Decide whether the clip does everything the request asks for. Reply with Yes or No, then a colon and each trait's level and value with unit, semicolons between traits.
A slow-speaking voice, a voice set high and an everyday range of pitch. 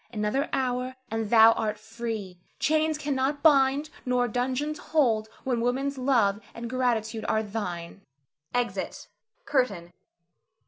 Yes: slow, 120 wpm; high, 245 Hz; average, 3.6 semitones